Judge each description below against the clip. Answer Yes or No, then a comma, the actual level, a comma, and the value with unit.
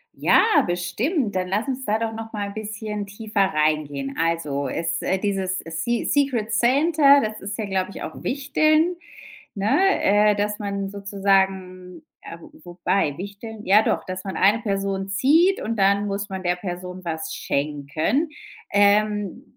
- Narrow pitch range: No, average, 3.3 semitones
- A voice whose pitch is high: Yes, high, 200 Hz